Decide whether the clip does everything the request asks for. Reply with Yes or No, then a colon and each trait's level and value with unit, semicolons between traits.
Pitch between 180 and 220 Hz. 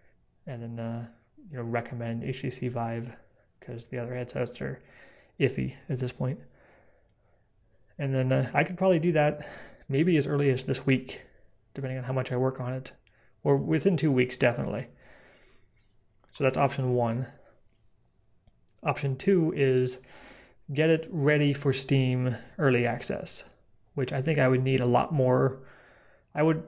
No: low, 130 Hz